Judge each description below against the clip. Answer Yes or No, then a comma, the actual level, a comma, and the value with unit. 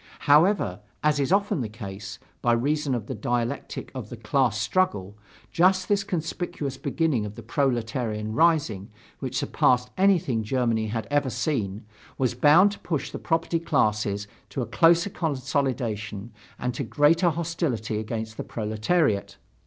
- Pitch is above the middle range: No, low, 130 Hz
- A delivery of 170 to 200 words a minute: No, average, 145 wpm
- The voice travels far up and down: Yes, wide, 6.6 semitones